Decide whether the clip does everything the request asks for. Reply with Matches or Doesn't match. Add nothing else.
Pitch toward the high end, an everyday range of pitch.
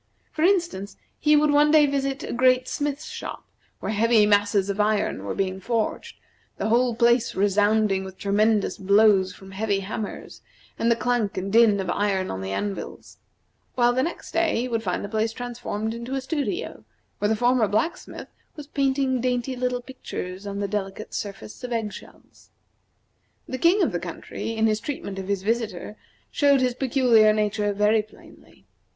Matches